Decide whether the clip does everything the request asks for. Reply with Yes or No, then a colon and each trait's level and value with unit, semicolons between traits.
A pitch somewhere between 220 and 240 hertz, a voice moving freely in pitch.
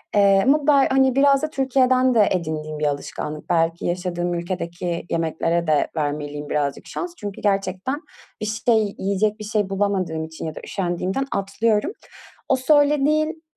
No: high, 195 Hz; wide, 7.5 semitones